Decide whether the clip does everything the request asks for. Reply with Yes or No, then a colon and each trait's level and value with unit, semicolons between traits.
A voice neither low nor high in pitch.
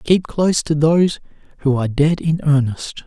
Yes: medium, 155 Hz